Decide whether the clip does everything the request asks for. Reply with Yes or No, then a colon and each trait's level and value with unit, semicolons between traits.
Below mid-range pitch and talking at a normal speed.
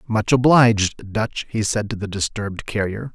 Yes: low, 110 Hz; average, 170 wpm